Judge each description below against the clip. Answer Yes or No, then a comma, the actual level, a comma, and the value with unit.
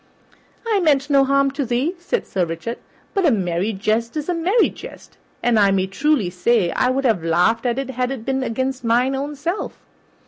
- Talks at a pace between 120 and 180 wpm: No, fast, 205 wpm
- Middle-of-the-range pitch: No, very high, 255 Hz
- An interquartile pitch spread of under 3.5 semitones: No, average, 4.5 semitones